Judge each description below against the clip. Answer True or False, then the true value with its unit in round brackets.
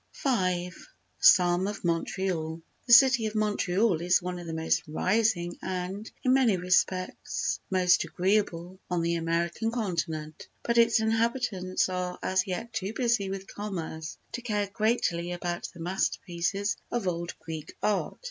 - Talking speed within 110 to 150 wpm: True (145 wpm)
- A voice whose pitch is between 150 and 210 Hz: True (185 Hz)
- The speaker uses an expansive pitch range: False (3.8 semitones)